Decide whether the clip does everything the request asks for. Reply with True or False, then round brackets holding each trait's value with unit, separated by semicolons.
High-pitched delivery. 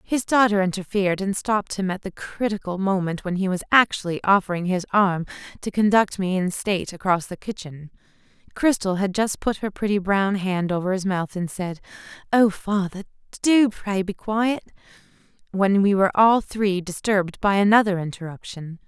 True (195 Hz)